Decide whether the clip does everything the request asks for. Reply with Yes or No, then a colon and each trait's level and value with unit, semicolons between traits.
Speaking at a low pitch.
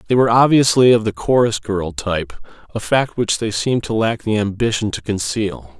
Yes: low, 110 Hz